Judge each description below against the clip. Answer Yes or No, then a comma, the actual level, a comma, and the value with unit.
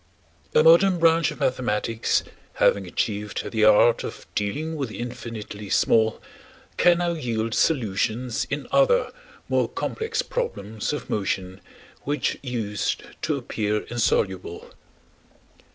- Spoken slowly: Yes, slow, 120 wpm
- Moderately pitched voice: No, low, 115 Hz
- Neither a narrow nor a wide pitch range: No, wide, 7.1 semitones